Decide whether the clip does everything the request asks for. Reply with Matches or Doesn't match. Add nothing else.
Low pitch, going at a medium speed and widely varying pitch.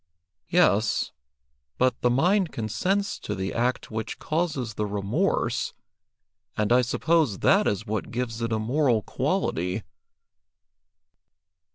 Doesn't match